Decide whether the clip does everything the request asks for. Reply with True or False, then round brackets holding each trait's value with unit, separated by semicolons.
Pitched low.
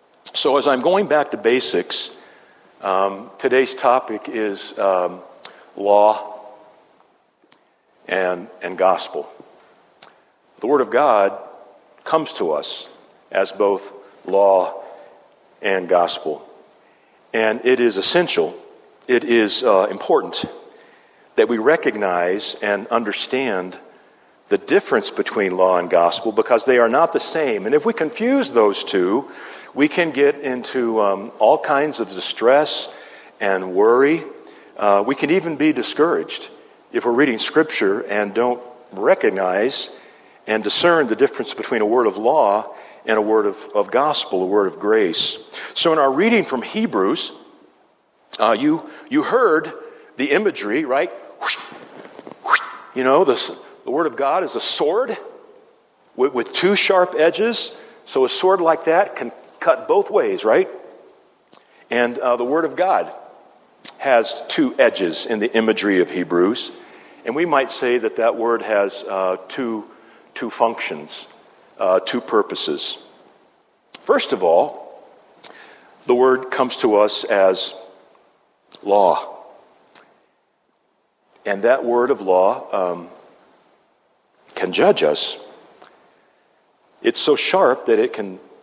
False (175 Hz)